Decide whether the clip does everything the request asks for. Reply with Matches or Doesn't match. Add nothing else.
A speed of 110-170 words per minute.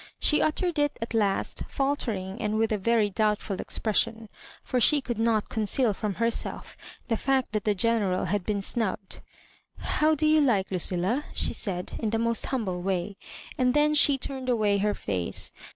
Doesn't match